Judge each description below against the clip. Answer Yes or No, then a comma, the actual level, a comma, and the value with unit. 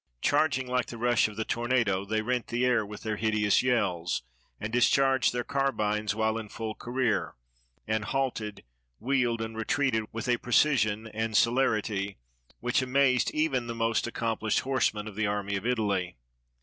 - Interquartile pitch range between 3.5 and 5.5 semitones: No, average, 2.9 semitones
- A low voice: Yes, low, 115 Hz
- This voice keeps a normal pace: Yes, average, 160 wpm